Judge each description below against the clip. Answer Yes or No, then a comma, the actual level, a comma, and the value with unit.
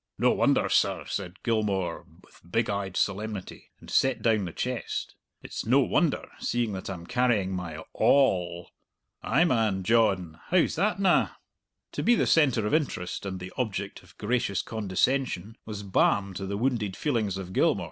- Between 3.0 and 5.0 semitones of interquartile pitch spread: Yes, average, 4.7 semitones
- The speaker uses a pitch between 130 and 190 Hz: No, low, 105 Hz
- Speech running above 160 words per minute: Yes, average, 170 wpm